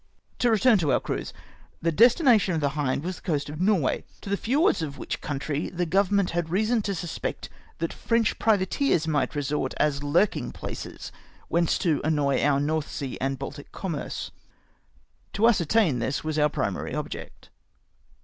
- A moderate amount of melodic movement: No, wide, 5.7 semitones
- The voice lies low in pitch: No, medium, 165 Hz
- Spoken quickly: No, average, 175 wpm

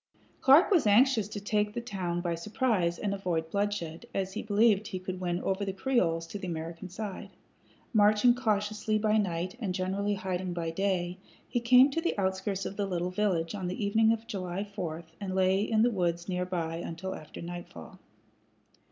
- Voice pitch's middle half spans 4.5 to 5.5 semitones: No, average, 3.1 semitones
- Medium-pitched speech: No, high, 195 Hz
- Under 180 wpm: No, average, 185 wpm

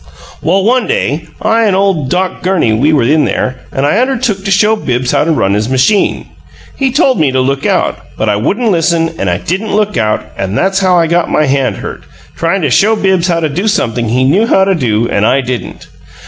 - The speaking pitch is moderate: Yes, medium, 165 Hz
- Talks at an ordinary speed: No, fast, 230 wpm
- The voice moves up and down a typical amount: No, wide, 7.3 semitones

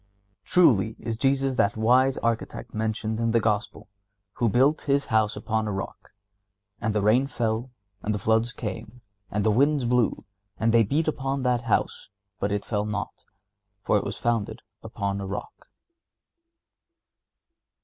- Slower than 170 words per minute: Yes, average, 155 wpm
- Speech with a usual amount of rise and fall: Yes, average, 3.1 semitones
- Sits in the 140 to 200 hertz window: No, low, 115 Hz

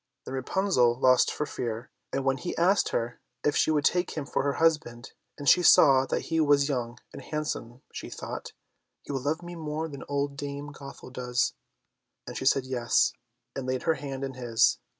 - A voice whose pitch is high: No, medium, 140 Hz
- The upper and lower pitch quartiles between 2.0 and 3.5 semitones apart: Yes, average, 3.0 semitones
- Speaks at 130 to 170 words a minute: No, average, 195 wpm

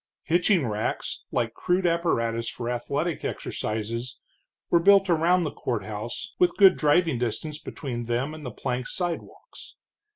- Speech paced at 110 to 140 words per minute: Yes, slow, 135 wpm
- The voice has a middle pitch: Yes, medium, 150 Hz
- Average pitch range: No, wide, 6.6 semitones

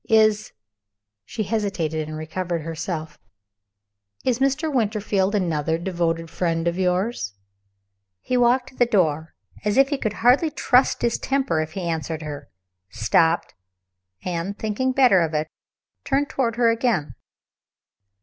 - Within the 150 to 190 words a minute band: No, average, 140 wpm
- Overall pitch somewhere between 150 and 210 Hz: Yes, high, 190 Hz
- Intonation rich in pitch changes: Yes, wide, 6.7 semitones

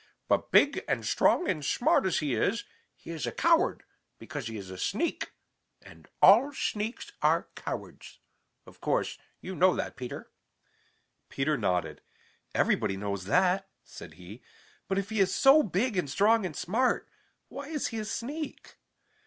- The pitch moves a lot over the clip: Yes, wide, 8.8 semitones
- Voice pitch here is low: No, high, 190 Hz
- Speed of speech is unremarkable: Yes, average, 160 wpm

